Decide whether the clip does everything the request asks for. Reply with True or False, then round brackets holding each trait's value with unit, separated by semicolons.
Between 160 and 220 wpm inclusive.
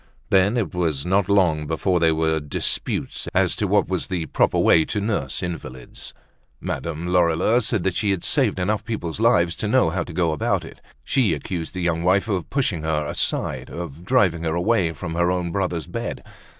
True (190 wpm)